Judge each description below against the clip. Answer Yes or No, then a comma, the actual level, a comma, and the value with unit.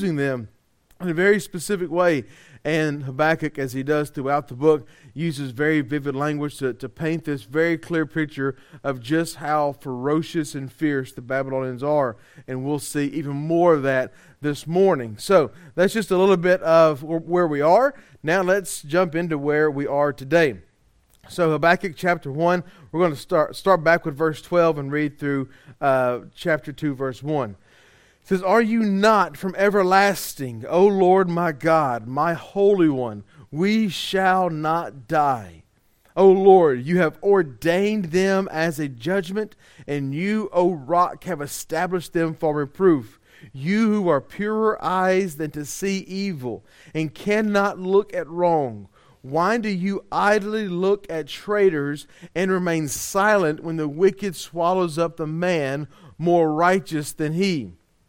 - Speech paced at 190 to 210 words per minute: No, average, 155 wpm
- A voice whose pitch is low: No, medium, 160 Hz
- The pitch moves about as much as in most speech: Yes, average, 4.5 semitones